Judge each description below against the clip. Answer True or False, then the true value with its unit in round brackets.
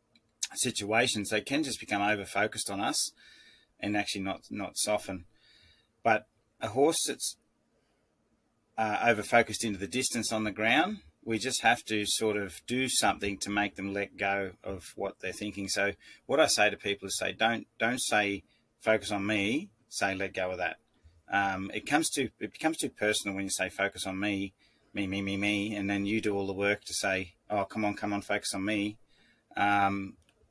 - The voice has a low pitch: True (100 Hz)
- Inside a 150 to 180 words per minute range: False (195 wpm)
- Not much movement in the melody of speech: True (1.6 semitones)